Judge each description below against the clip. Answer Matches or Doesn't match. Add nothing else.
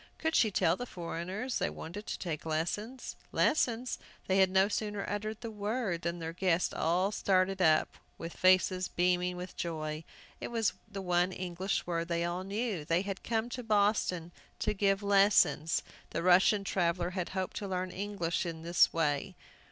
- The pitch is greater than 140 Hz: Matches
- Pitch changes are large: Doesn't match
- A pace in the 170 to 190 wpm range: Matches